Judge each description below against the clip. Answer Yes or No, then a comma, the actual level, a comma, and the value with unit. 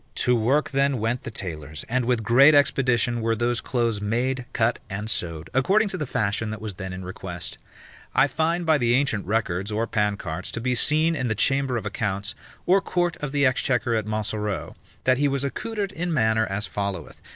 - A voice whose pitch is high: No, low, 120 Hz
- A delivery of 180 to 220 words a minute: Yes, average, 195 wpm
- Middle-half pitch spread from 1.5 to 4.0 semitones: No, average, 4.8 semitones